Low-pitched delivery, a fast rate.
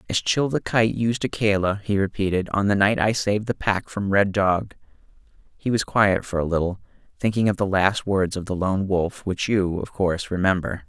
Yes: low, 100 Hz; fast, 210 wpm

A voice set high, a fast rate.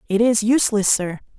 No: high, 215 Hz; average, 175 wpm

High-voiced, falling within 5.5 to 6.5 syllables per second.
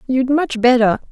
No: very high, 250 Hz; 4.6 syllables/s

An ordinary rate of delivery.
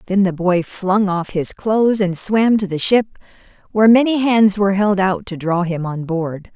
No: fast, 210 wpm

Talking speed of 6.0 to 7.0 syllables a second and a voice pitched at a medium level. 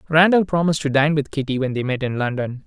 Yes: 6.4 syllables/s; medium, 145 Hz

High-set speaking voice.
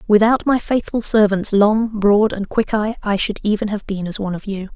Yes: high, 210 Hz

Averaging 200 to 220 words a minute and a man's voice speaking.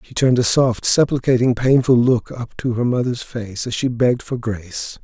Yes: fast, 205 wpm; male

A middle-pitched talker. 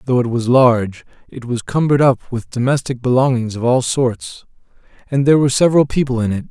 No: low, 125 Hz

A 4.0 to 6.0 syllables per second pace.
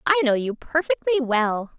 Yes: 5.2 syllables/s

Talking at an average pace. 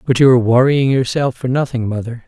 Yes: average, 185 wpm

